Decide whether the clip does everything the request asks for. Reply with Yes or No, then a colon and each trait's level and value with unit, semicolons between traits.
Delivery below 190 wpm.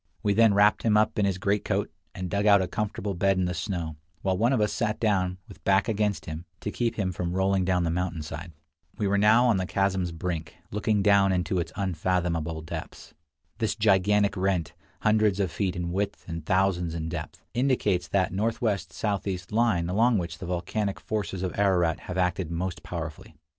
No: average, 195 wpm